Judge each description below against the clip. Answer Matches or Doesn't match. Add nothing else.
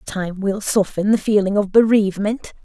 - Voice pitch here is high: Matches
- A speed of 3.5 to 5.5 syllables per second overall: Matches